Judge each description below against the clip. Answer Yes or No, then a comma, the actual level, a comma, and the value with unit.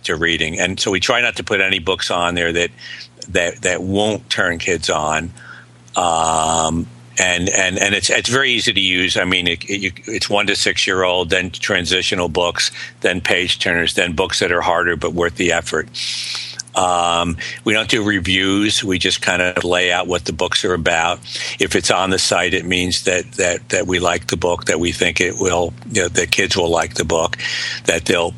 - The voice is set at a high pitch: No, very low, 90 Hz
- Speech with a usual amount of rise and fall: No, narrow, 1.8 semitones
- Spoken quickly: Yes, fast, 210 wpm